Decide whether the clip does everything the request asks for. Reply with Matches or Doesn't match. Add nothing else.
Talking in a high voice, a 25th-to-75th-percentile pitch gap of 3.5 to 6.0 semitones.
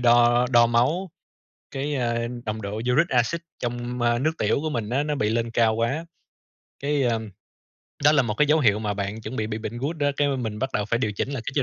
Doesn't match